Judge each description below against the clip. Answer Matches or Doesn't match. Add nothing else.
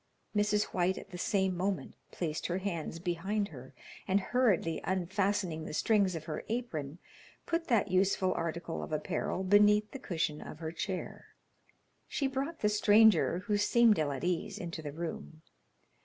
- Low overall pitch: Doesn't match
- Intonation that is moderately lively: Matches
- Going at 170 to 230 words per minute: Doesn't match